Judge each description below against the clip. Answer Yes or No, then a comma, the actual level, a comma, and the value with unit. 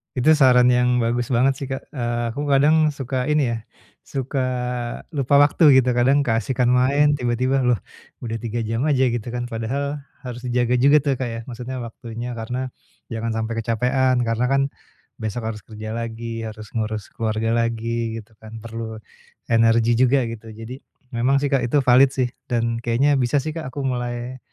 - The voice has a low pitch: Yes, low, 120 Hz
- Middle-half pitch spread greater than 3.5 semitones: No, narrow, 2.6 semitones